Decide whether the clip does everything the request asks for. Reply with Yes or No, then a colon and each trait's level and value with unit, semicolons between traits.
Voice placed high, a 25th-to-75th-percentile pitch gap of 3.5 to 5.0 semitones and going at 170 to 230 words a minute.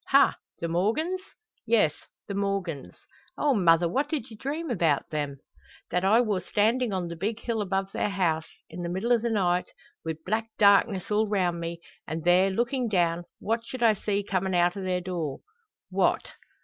Yes: high, 195 Hz; average, 4.5 semitones; average, 185 wpm